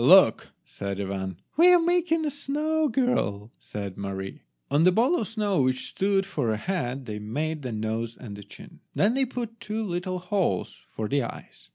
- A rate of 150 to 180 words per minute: No, average, 190 wpm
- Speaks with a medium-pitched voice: Yes, medium, 165 Hz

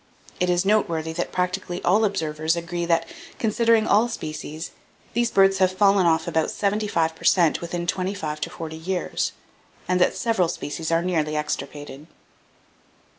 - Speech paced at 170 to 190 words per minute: No, average, 155 wpm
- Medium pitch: Yes, medium, 175 Hz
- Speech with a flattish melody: No, average, 3.3 semitones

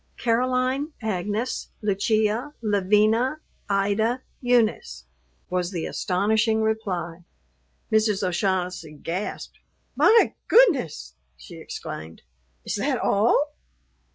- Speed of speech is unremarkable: No, slow, 85 wpm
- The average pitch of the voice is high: Yes, high, 210 Hz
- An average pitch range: Yes, average, 4.5 semitones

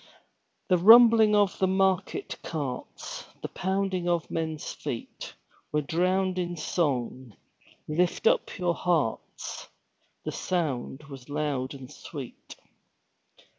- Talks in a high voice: No, medium, 170 Hz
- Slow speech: Yes, slow, 110 wpm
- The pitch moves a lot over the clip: No, average, 4.7 semitones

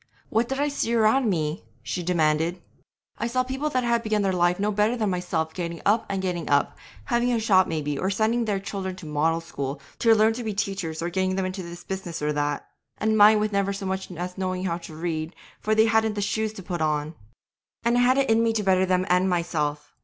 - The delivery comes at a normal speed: No, fast, 235 wpm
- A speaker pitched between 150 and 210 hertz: Yes, high, 190 Hz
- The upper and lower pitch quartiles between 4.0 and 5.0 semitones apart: Yes, average, 4.4 semitones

